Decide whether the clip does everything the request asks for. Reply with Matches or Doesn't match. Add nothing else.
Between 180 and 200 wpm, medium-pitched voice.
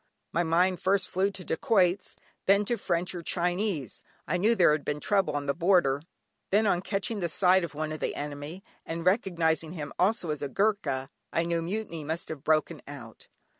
Matches